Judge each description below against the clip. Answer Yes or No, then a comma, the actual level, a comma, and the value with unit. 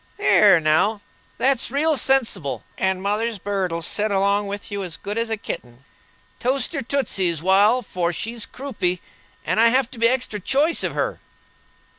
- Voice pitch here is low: No, high, 210 Hz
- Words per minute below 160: No, average, 165 wpm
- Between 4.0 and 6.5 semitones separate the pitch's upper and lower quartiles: Yes, average, 4.9 semitones